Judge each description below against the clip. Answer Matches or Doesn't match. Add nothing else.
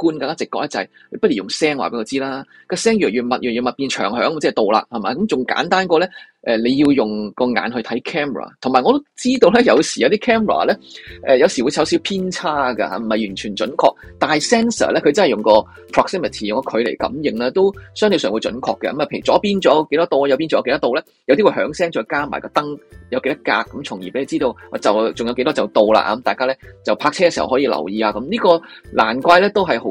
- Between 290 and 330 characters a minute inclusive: Doesn't match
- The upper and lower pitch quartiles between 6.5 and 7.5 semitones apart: Matches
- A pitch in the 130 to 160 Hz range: Matches